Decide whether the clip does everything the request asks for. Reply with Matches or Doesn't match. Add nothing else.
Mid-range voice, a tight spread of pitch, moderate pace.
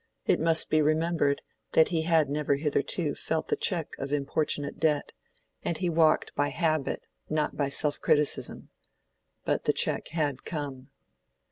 Matches